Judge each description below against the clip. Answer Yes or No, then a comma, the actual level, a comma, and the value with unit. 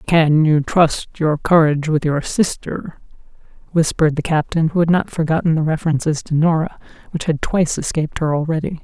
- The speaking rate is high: No, average, 170 wpm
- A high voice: No, medium, 160 Hz